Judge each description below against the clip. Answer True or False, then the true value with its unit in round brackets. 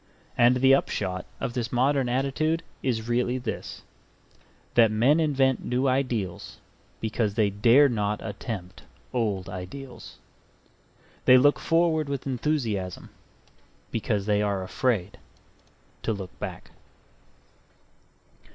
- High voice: False (120 Hz)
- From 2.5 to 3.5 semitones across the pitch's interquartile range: False (4.5 semitones)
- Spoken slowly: True (110 wpm)